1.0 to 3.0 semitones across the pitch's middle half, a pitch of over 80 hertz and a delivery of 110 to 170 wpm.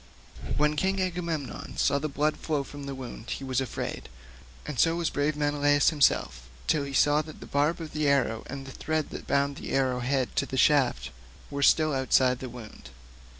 No: narrow, 2.5 semitones; medium, 140 Hz; average, 195 wpm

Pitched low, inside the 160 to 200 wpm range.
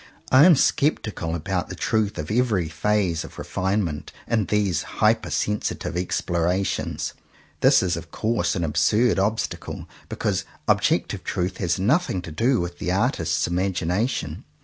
No: very low, 95 Hz; average, 145 wpm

